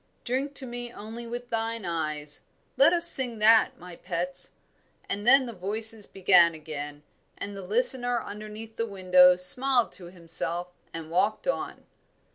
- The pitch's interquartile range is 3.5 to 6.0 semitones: Yes, average, 5.1 semitones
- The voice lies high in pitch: Yes, high, 210 Hz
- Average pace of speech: Yes, average, 150 wpm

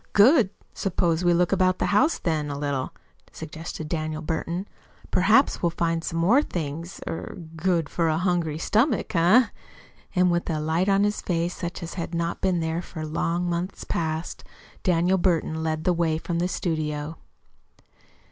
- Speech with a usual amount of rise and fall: No, narrow, 2.2 semitones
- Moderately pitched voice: Yes, medium, 170 Hz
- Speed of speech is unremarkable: Yes, average, 165 wpm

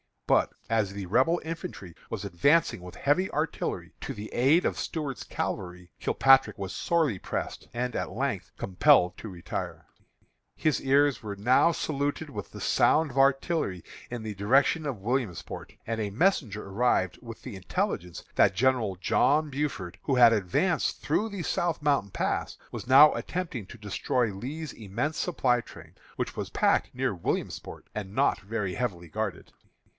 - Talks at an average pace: Yes, average, 160 wpm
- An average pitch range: No, wide, 6.5 semitones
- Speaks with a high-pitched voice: No, low, 120 Hz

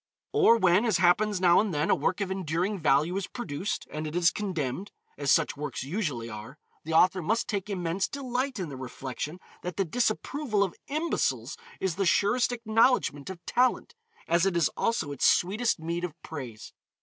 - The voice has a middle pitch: Yes, medium, 180 Hz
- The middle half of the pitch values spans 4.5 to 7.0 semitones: Yes, wide, 5.4 semitones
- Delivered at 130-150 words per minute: No, average, 185 wpm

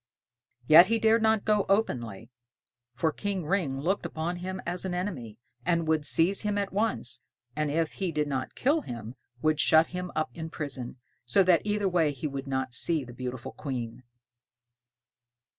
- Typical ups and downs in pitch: No, wide, 6.1 semitones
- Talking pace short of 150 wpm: No, average, 175 wpm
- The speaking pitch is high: No, medium, 160 Hz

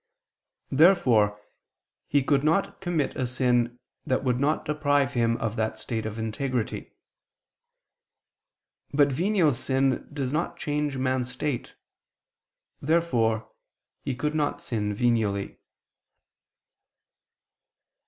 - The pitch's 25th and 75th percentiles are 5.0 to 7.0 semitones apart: No, average, 4.2 semitones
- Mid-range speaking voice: No, low, 130 Hz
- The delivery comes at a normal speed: No, slow, 105 wpm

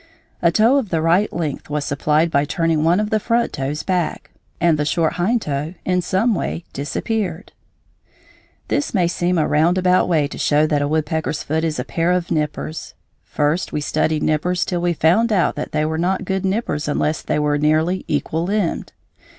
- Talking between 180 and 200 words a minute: Yes, average, 190 wpm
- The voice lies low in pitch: No, medium, 165 Hz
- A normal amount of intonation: Yes, average, 3.3 semitones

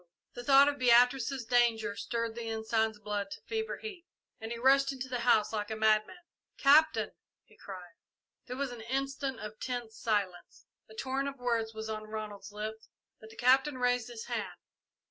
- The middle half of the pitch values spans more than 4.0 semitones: No, average, 3.5 semitones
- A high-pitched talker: Yes, high, 235 Hz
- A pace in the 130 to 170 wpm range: No, average, 180 wpm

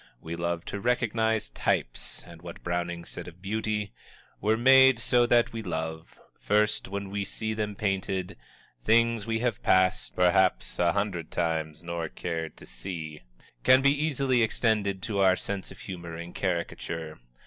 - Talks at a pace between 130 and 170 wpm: Yes, average, 160 wpm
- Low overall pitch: Yes, very low, 95 Hz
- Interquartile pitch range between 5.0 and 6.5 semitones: No, average, 4.6 semitones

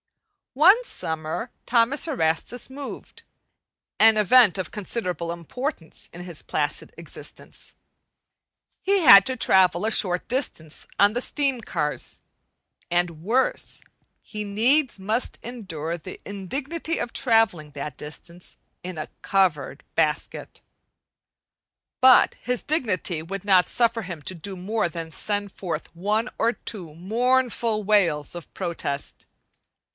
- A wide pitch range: Yes, wide, 5.9 semitones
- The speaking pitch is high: Yes, high, 200 Hz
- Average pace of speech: No, slow, 120 wpm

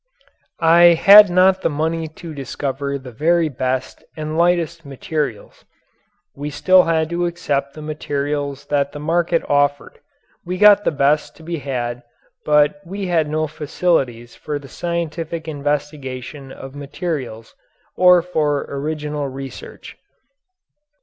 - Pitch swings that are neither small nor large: Yes, average, 3.3 semitones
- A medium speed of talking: No, slow, 130 wpm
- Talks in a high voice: No, medium, 150 Hz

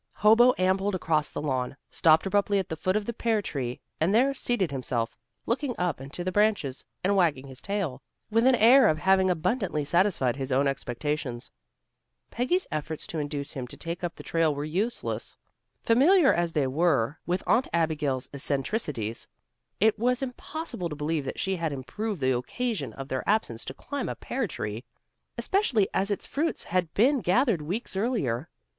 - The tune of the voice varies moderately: No, wide, 7.5 semitones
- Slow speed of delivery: No, average, 180 wpm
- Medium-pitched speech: Yes, medium, 175 Hz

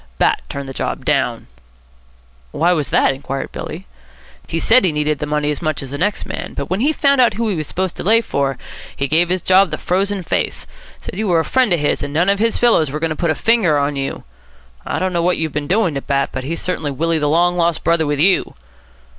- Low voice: No, medium, 165 Hz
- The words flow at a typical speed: No, fast, 250 wpm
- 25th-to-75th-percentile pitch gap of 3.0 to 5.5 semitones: Yes, average, 4.2 semitones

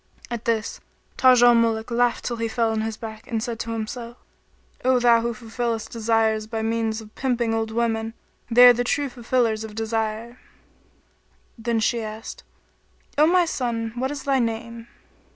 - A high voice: Yes, high, 230 Hz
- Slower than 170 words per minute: No, average, 175 wpm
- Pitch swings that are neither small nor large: No, narrow, 1.4 semitones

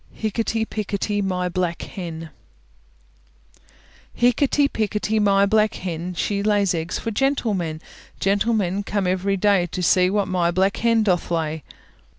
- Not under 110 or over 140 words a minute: Yes, slow, 135 wpm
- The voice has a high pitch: Yes, high, 195 Hz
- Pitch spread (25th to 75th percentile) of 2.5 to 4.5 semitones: Yes, average, 3.0 semitones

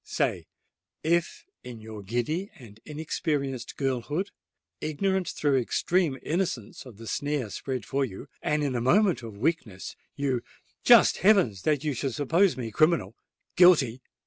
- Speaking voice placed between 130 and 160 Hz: Yes, medium, 140 Hz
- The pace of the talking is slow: Yes, slow, 120 wpm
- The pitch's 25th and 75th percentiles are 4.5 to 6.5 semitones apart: Yes, wide, 5.6 semitones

